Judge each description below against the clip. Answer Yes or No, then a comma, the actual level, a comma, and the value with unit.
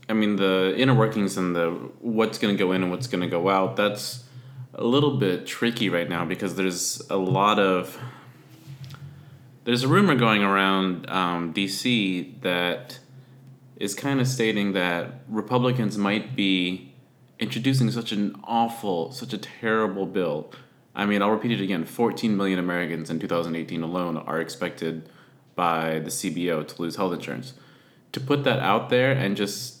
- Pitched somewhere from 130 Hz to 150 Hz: No, low, 100 Hz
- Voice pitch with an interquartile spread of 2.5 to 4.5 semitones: No, wide, 5.6 semitones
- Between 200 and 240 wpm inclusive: No, average, 165 wpm